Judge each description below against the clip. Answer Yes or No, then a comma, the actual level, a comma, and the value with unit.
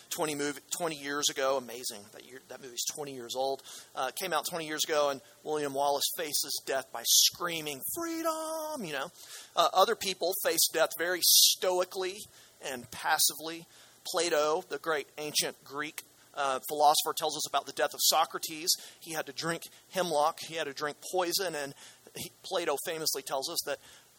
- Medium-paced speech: Yes, average, 170 wpm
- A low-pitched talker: No, medium, 155 Hz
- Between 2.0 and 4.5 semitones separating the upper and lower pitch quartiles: Yes, average, 3.6 semitones